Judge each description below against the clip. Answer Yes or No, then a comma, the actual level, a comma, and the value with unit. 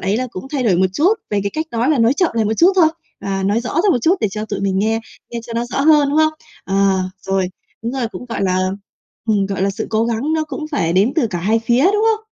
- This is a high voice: Yes, high, 230 Hz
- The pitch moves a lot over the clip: Yes, wide, 6.7 semitones